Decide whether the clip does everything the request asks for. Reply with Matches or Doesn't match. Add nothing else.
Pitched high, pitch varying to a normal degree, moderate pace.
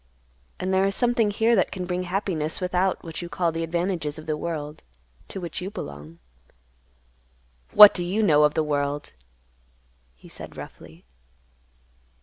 Doesn't match